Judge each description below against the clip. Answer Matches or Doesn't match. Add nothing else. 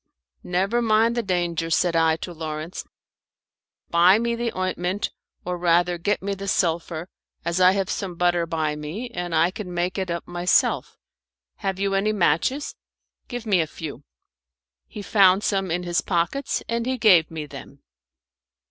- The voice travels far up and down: Doesn't match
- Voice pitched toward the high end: Doesn't match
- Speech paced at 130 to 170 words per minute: Matches